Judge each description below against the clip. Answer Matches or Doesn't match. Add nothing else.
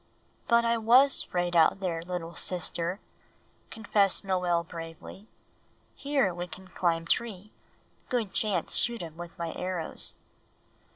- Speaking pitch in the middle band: Matches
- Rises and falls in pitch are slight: Doesn't match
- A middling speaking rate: Doesn't match